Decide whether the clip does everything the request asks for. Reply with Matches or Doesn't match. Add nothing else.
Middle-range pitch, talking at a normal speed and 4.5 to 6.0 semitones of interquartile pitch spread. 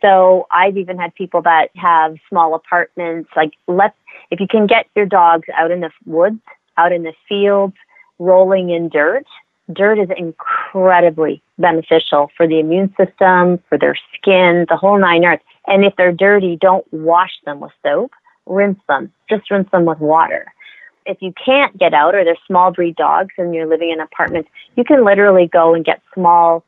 Doesn't match